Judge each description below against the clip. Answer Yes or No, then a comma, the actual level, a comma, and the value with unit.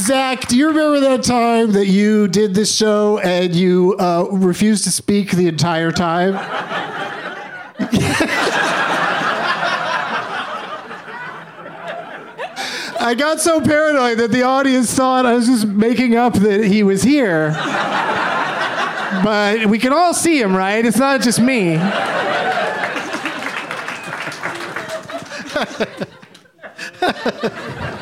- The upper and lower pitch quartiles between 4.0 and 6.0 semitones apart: Yes, average, 4.8 semitones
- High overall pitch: Yes, high, 220 Hz